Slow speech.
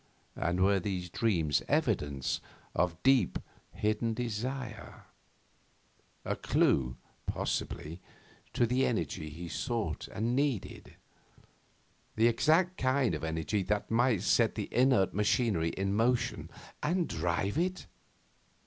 Yes: slow, 115 wpm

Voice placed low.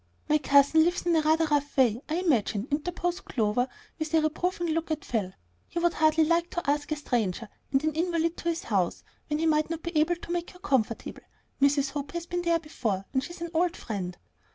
No: very high, 310 Hz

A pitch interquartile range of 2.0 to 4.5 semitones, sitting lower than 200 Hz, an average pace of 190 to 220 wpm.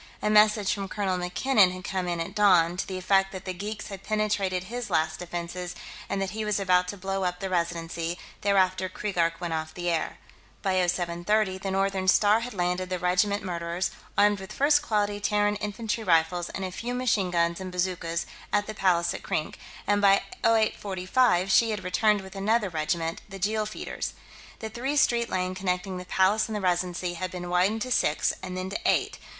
Yes: narrow, 2.6 semitones; high, 190 Hz; average, 200 wpm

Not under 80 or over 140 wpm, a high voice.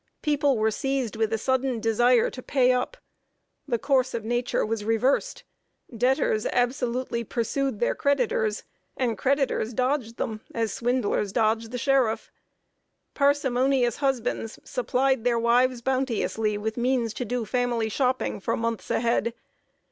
Yes: slow, 135 wpm; high, 245 Hz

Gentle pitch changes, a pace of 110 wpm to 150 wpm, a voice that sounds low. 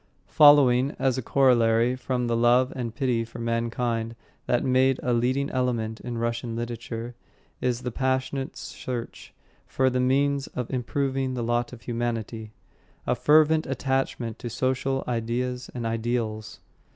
Yes: narrow, 2.1 semitones; average, 140 wpm; low, 125 Hz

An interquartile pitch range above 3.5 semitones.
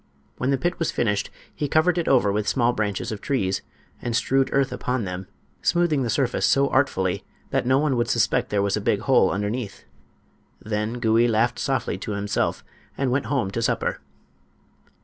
Yes: average, 4.5 semitones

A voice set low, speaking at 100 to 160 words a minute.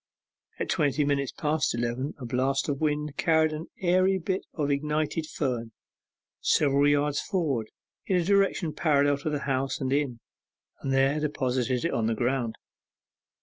No: medium, 145 Hz; average, 155 wpm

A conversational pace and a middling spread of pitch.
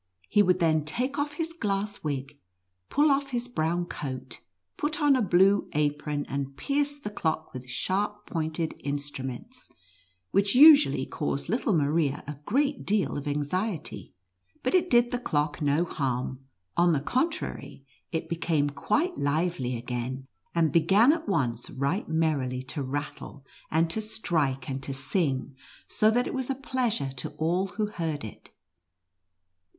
No: average, 155 wpm; wide, 7.7 semitones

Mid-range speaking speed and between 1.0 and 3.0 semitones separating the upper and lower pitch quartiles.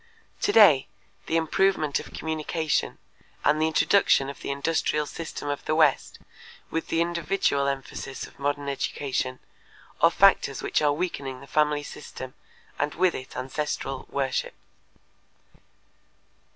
No: slow, 125 wpm; narrow, 2.6 semitones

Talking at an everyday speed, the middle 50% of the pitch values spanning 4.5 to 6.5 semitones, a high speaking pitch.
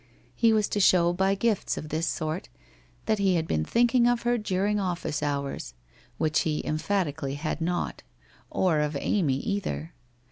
No: average, 170 wpm; average, 5.1 semitones; medium, 175 Hz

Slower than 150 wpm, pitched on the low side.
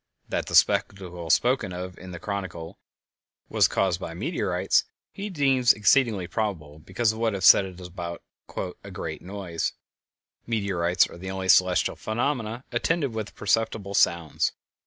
Yes: average, 140 wpm; very low, 95 Hz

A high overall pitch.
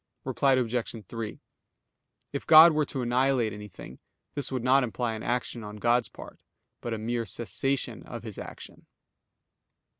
No: low, 120 Hz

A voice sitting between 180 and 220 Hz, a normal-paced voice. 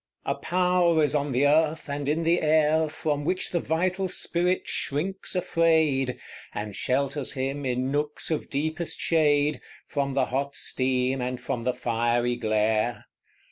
No: medium, 145 Hz; average, 150 wpm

